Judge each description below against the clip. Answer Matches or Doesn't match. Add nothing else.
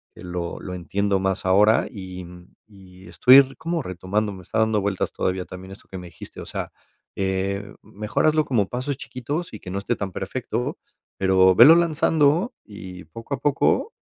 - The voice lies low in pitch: Matches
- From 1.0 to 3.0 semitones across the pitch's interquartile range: Doesn't match